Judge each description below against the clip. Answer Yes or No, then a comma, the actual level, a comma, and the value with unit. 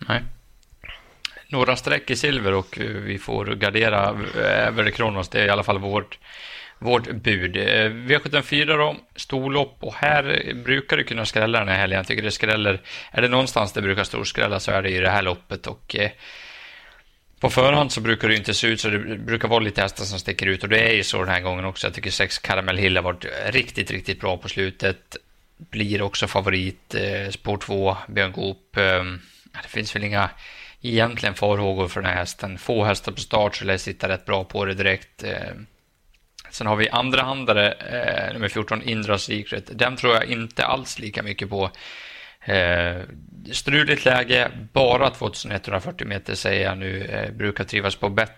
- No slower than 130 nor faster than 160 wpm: No, average, 185 wpm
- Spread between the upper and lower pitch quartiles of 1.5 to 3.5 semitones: Yes, average, 2.9 semitones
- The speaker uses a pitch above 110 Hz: No, low, 105 Hz